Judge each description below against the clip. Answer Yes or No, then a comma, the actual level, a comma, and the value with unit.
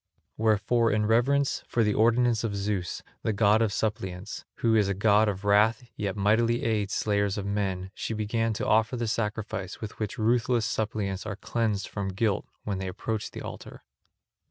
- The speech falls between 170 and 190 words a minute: Yes, average, 180 wpm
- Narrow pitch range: Yes, narrow, 2.0 semitones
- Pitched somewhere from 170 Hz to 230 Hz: No, low, 105 Hz